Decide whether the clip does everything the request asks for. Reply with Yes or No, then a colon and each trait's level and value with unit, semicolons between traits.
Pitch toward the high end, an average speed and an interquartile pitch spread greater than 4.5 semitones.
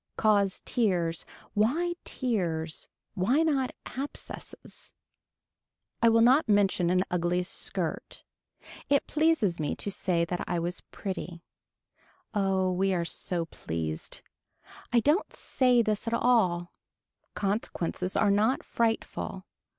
No: high, 200 Hz; slow, 115 wpm; average, 4.9 semitones